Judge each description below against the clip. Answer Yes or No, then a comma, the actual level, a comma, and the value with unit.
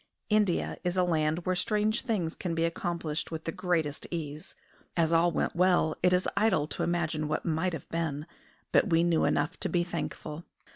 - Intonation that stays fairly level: Yes, narrow, 2.3 semitones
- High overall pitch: No, medium, 170 Hz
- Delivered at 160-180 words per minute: No, average, 190 wpm